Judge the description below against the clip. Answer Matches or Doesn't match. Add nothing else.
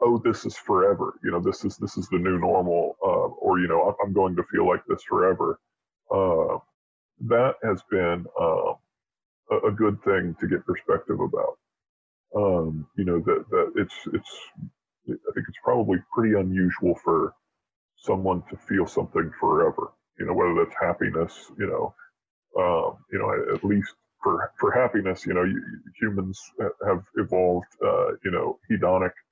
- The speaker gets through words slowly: Doesn't match